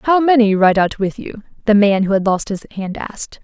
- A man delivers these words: No, female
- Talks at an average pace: No, fast, 245 wpm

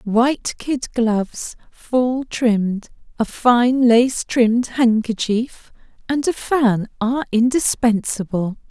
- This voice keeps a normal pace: No, slow, 105 wpm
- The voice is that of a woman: Yes, female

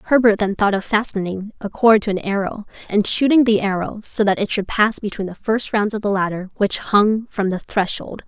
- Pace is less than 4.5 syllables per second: No, 5.2 syllables/s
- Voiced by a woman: Yes, female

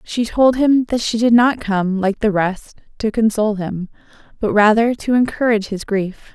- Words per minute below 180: No, average, 190 wpm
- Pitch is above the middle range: Yes, high, 220 Hz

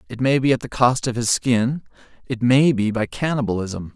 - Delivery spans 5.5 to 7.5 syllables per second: No, 5.1 syllables/s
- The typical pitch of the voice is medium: No, low, 120 Hz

